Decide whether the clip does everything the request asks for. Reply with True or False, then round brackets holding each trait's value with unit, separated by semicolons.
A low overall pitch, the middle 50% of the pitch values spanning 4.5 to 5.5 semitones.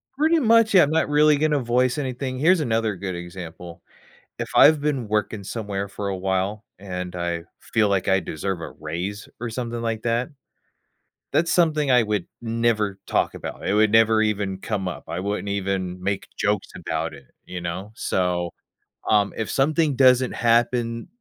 True (110 Hz; 5.0 semitones)